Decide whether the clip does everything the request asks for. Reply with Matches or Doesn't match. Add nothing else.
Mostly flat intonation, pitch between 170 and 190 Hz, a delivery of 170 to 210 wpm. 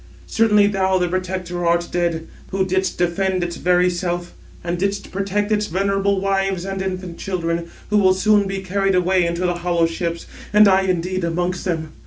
Matches